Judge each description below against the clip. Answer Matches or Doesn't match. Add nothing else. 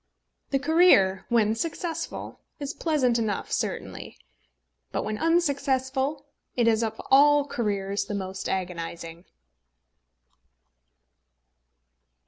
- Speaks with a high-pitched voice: Matches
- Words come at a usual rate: Doesn't match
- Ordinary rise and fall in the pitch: Doesn't match